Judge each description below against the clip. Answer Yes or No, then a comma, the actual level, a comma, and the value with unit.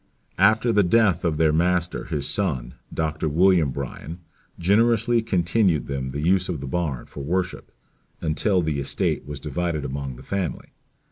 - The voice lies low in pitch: Yes, very low, 85 Hz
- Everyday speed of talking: Yes, average, 155 wpm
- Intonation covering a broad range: No, average, 4.7 semitones